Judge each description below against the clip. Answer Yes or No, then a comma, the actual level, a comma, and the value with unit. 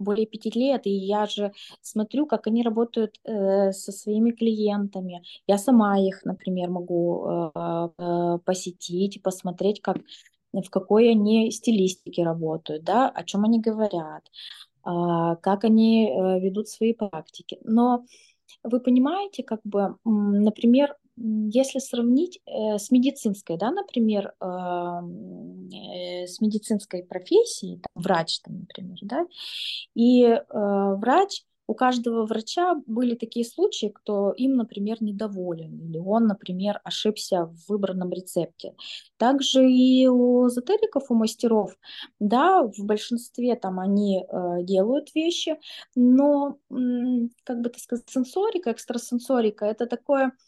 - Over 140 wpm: No, average, 115 wpm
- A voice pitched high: Yes, high, 215 Hz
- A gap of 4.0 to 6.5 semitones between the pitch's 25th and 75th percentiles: Yes, average, 4.4 semitones